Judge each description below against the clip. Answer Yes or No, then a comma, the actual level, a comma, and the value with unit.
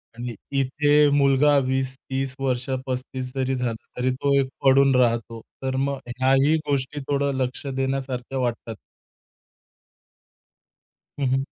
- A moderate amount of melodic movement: No, narrow, 1.3 semitones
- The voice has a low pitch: Yes, low, 130 Hz